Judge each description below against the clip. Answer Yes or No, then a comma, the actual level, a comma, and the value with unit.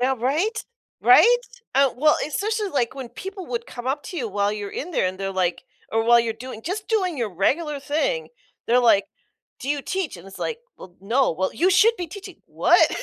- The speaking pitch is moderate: No, very high, 270 Hz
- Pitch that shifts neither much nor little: No, wide, 8.6 semitones